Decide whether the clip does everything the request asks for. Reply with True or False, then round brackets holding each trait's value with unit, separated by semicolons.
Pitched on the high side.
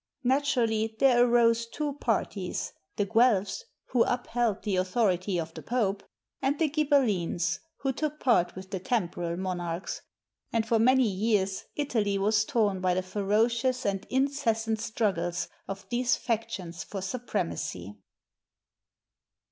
True (220 Hz)